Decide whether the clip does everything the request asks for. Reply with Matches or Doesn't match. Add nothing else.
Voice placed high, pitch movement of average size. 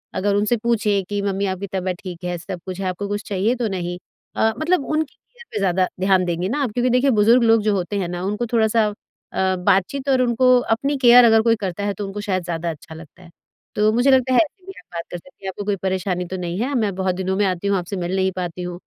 Matches